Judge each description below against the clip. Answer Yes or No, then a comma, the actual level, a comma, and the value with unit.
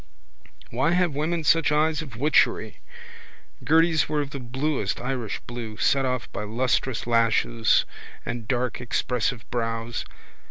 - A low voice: Yes, low, 125 Hz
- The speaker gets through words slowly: Yes, slow, 130 wpm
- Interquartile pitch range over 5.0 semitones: No, average, 4.4 semitones